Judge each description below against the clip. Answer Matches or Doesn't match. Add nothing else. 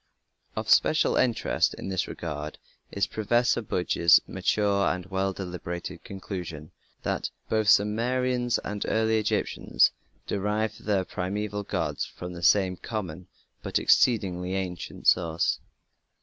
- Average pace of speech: Doesn't match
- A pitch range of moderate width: Matches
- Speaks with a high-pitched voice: Doesn't match